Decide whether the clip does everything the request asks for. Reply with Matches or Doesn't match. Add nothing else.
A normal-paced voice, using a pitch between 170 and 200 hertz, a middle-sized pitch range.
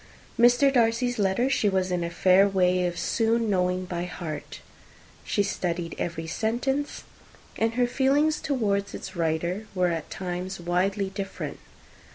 Matches